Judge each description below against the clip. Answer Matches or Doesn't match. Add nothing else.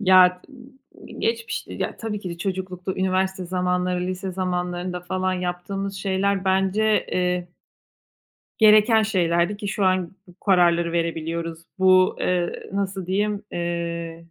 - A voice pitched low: Doesn't match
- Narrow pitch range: Matches